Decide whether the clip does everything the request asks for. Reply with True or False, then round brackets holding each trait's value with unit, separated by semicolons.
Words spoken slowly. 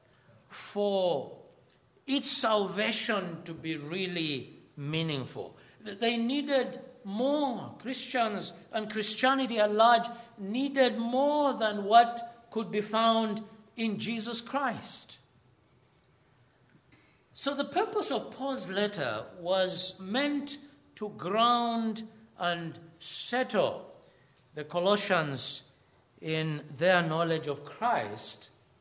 True (90 wpm)